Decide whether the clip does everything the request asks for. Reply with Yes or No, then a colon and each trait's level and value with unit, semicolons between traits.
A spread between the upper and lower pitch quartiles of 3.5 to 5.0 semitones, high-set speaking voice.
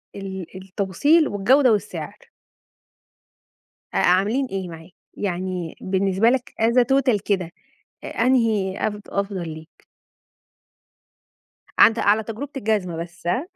Yes: average, 3.9 semitones; high, 200 Hz